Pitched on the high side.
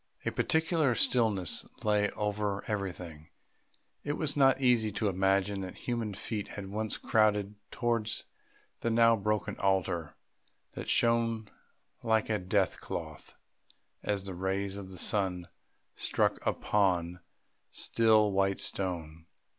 No: low, 105 Hz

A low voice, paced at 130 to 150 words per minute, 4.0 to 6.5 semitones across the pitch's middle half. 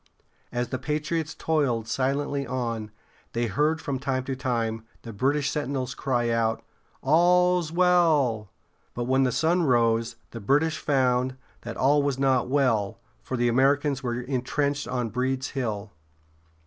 No: low, 130 Hz; average, 145 wpm; average, 3.3 semitones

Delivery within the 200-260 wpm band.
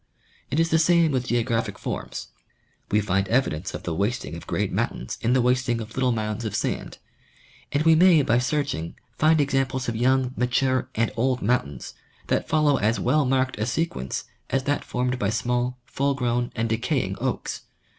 No: average, 185 wpm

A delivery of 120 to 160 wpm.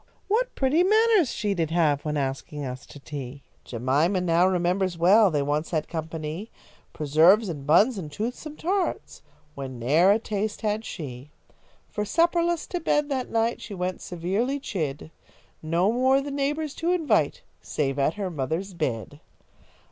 Yes: average, 155 wpm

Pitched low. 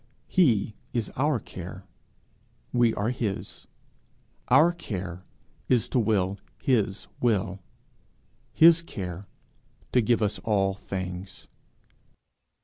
Yes: low, 105 Hz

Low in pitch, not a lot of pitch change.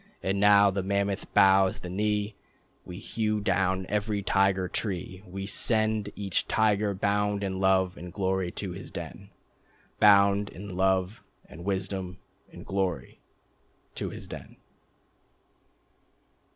Yes: low, 100 Hz; narrow, 1.5 semitones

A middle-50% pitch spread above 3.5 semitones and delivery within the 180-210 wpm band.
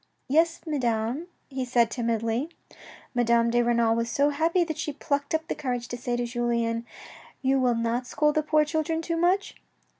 Yes: average, 4.7 semitones; average, 190 wpm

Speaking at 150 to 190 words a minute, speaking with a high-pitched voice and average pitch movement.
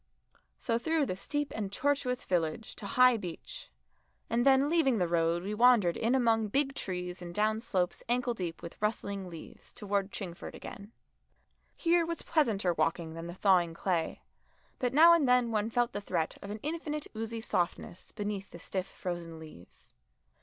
No: average, 170 wpm; high, 210 Hz; wide, 5.9 semitones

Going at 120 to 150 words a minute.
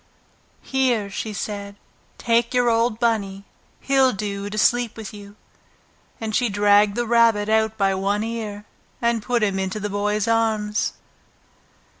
Yes: average, 145 wpm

